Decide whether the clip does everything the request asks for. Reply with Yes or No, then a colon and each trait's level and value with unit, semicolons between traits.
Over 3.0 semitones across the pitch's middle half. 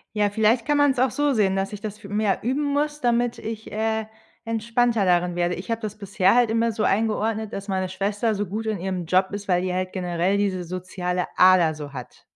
Yes: average, 3.5 semitones